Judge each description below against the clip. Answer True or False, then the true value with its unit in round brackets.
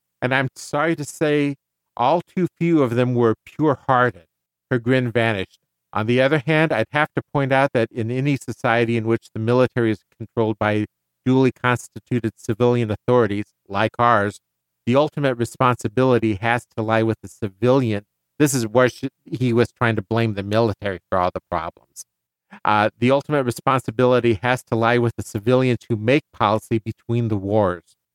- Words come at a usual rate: True (175 wpm)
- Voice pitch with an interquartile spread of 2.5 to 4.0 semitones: True (2.9 semitones)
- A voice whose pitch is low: True (120 Hz)